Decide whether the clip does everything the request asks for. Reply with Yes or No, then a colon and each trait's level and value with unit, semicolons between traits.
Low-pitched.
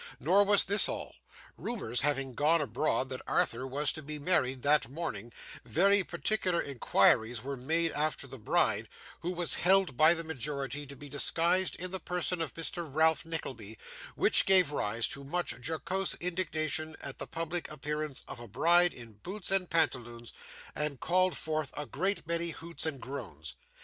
No: medium, 155 Hz